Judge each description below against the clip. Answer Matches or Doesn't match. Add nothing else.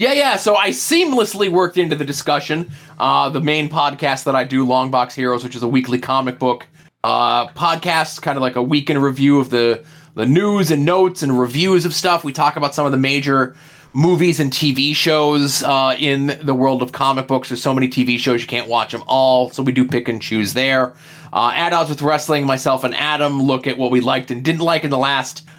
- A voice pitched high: Doesn't match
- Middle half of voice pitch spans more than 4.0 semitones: Doesn't match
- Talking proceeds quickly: Matches